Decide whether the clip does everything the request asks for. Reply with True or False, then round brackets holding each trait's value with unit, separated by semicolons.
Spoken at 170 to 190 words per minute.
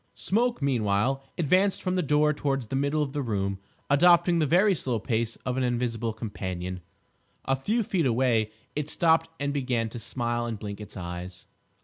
True (175 wpm)